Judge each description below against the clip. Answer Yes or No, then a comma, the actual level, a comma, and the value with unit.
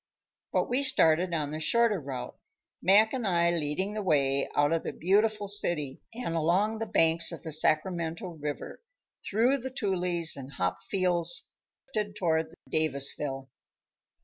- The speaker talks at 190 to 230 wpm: No, average, 145 wpm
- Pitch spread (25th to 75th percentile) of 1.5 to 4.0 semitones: No, average, 5.0 semitones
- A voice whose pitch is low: No, medium, 170 Hz